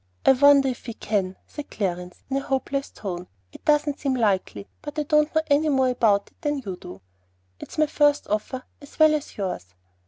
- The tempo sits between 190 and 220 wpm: Yes, fast, 205 wpm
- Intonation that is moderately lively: No, wide, 6.6 semitones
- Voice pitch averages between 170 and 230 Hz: No, very high, 265 Hz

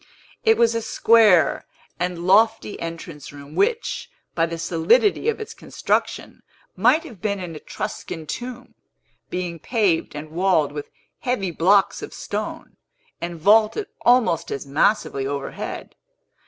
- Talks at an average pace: No, slow, 130 wpm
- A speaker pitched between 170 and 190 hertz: Yes, medium, 185 Hz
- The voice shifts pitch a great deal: Yes, wide, 5.8 semitones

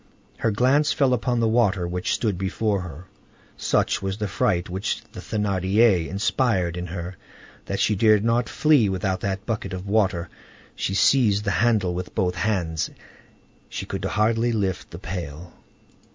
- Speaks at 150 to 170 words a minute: Yes, average, 160 wpm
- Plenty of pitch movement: No, average, 3.6 semitones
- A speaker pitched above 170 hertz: No, low, 100 Hz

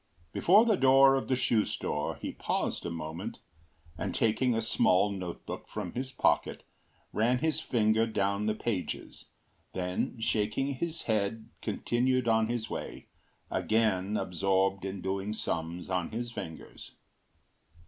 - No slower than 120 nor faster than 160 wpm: Yes, average, 140 wpm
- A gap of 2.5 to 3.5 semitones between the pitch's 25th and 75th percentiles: No, average, 4.2 semitones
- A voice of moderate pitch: No, low, 110 Hz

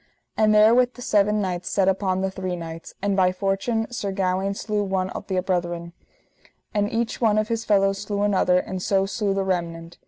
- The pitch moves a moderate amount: No, narrow, 2.3 semitones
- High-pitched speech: Yes, high, 195 Hz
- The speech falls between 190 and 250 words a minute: Yes, average, 195 wpm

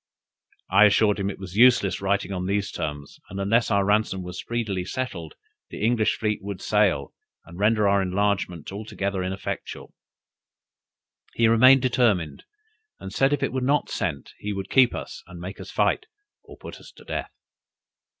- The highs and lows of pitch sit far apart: No, average, 3.1 semitones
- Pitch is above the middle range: No, low, 100 Hz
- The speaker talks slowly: No, average, 170 wpm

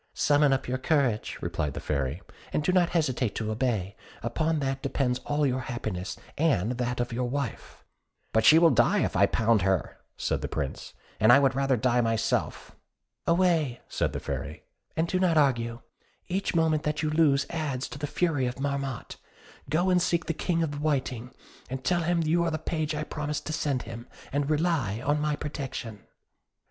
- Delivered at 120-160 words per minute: No, average, 190 wpm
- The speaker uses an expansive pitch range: No, average, 4.6 semitones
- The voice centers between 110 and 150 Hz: Yes, medium, 140 Hz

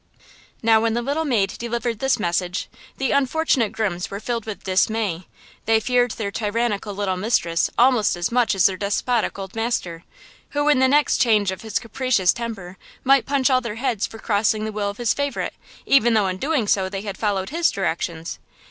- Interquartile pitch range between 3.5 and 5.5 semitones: Yes, average, 4.0 semitones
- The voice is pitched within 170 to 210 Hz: No, high, 220 Hz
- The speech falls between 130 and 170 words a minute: No, average, 190 wpm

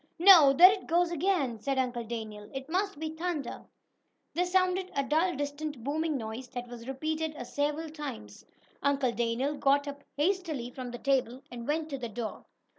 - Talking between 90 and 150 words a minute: No, average, 175 wpm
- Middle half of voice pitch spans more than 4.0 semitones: Yes, average, 4.6 semitones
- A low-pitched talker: No, very high, 285 Hz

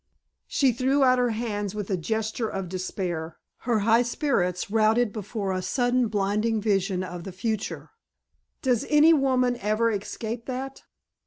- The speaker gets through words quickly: No, average, 150 wpm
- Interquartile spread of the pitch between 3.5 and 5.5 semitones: Yes, average, 4.0 semitones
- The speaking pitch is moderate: No, high, 220 Hz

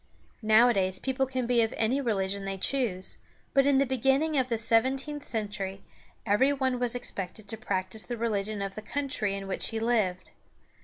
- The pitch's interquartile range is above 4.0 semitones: Yes, average, 4.8 semitones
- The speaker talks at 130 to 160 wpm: No, average, 175 wpm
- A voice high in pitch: Yes, high, 225 Hz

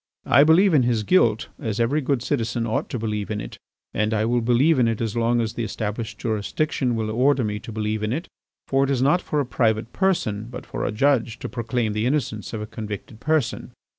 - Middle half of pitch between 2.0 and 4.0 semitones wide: Yes, average, 3.7 semitones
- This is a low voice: Yes, low, 115 Hz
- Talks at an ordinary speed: No, fast, 225 wpm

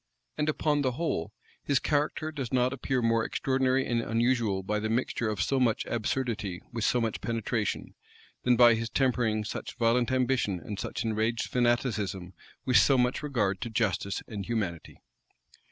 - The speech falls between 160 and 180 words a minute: Yes, average, 165 wpm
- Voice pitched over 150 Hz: No, low, 120 Hz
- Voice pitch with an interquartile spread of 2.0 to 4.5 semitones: Yes, average, 3.2 semitones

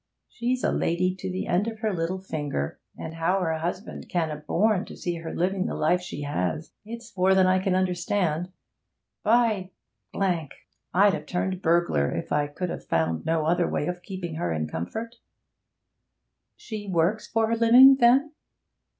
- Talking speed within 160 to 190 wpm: Yes, average, 175 wpm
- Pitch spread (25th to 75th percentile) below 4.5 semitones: Yes, average, 4.1 semitones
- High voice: No, medium, 180 Hz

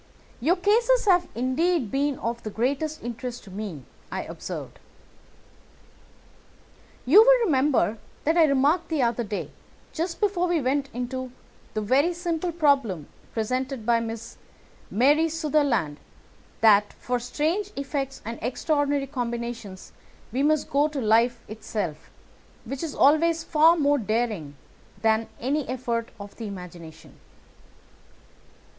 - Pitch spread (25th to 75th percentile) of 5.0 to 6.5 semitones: Yes, wide, 5.4 semitones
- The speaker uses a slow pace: Yes, slow, 125 wpm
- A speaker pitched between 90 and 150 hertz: No, very high, 260 Hz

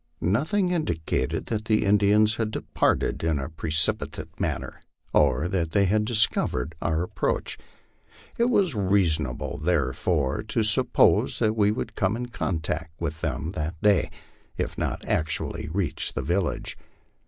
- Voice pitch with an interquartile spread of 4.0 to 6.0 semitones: Yes, average, 5.3 semitones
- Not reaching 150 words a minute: Yes, average, 140 wpm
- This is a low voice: Yes, very low, 90 Hz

